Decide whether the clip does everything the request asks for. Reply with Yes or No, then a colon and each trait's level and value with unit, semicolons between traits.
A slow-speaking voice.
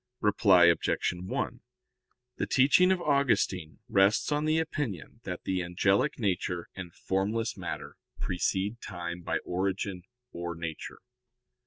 Yes: slow, 125 wpm